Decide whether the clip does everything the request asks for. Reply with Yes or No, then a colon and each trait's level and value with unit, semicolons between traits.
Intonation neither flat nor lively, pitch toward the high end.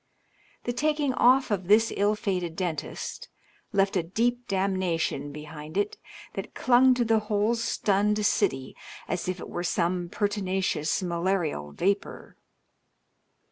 Yes: average, 3.9 semitones; high, 195 Hz